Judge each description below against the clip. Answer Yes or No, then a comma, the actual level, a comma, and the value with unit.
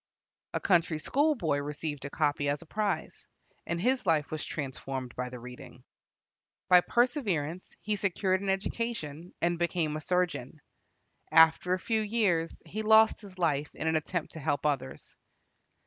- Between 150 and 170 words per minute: Yes, average, 155 wpm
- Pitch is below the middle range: No, medium, 165 Hz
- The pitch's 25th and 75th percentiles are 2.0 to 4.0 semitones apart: No, average, 5.3 semitones